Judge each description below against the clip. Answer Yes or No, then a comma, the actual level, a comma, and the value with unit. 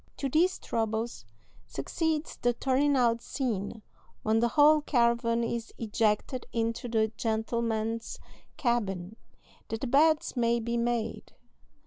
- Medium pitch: No, high, 235 Hz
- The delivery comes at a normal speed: No, slow, 120 wpm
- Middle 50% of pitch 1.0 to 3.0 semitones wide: Yes, narrow, 2.4 semitones